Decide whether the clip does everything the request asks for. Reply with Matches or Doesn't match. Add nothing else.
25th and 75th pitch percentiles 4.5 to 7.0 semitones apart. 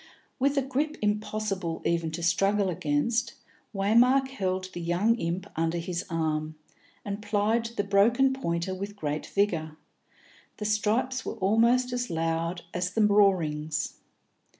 Matches